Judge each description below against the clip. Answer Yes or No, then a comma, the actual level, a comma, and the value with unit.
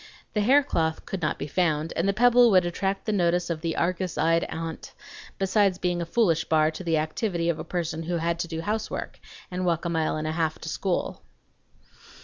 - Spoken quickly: Yes, fast, 210 wpm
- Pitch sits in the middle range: Yes, medium, 170 Hz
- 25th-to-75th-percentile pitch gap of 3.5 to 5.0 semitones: No, average, 2.7 semitones